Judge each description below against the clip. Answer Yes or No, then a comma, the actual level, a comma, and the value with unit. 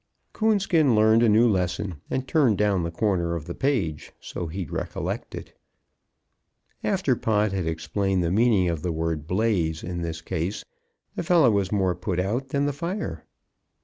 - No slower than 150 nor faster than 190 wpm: Yes, average, 170 wpm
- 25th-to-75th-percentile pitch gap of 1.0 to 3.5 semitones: No, wide, 5.5 semitones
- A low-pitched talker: Yes, very low, 95 Hz